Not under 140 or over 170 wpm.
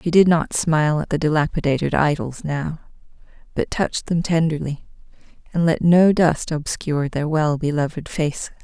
Yes: average, 155 wpm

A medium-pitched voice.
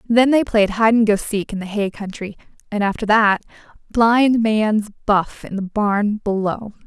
No: high, 210 Hz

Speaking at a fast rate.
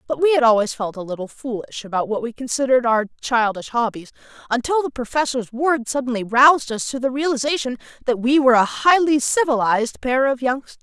No: average, 190 wpm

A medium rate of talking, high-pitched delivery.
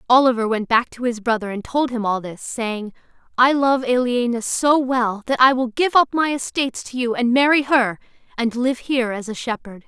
No: fast, 215 wpm; high, 245 Hz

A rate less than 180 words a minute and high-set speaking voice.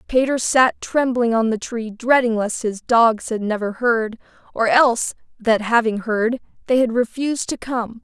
Yes: average, 170 wpm; high, 235 Hz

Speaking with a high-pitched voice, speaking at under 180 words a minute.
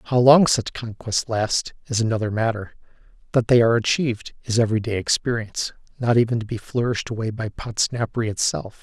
No: low, 115 Hz; average, 170 wpm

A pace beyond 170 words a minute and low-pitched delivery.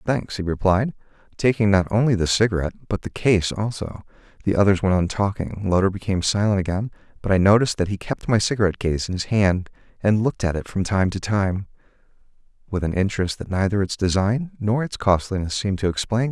Yes: average, 200 wpm; low, 100 Hz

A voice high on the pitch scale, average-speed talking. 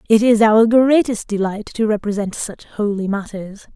Yes: high, 215 Hz; average, 160 wpm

